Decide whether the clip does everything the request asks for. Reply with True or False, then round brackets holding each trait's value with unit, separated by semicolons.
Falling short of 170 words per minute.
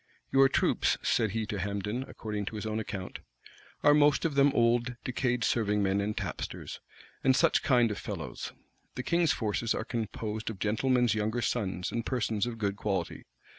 False (175 wpm)